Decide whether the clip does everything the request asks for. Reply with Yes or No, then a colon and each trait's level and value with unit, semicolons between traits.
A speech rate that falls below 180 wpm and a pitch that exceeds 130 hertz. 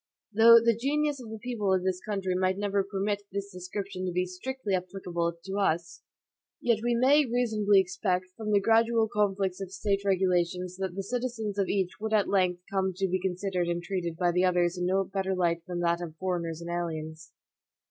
No: average, 200 wpm; high, 190 Hz